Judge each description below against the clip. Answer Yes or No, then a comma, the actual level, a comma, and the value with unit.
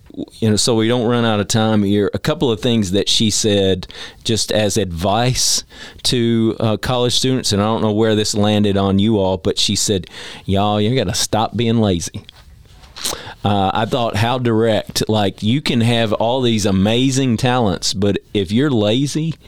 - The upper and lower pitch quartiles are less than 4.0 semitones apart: Yes, average, 2.7 semitones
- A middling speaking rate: Yes, average, 185 wpm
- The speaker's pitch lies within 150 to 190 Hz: No, low, 110 Hz